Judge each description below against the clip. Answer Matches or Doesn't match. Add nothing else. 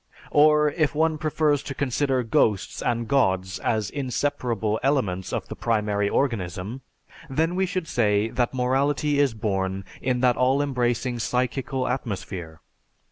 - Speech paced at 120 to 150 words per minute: Matches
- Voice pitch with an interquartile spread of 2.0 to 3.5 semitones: Doesn't match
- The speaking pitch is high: Doesn't match